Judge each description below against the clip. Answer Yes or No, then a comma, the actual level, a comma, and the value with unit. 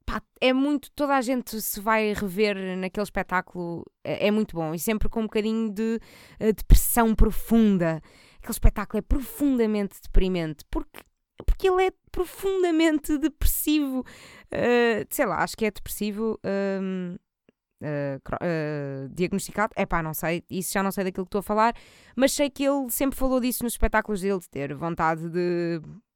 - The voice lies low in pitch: No, high, 210 Hz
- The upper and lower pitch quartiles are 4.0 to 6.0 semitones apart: Yes, wide, 5.4 semitones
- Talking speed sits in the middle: Yes, average, 165 wpm